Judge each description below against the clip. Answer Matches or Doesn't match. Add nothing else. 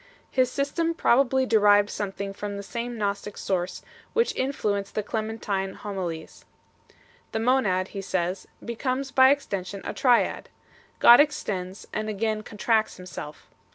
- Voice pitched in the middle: Doesn't match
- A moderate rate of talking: Matches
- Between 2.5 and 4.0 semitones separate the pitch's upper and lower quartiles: Doesn't match